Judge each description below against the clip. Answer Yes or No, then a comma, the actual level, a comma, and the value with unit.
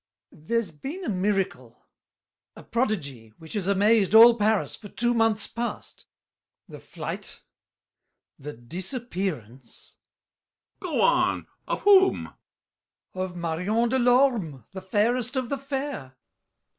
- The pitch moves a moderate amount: No, wide, 6.1 semitones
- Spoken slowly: Yes, slow, 120 wpm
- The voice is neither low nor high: No, high, 210 Hz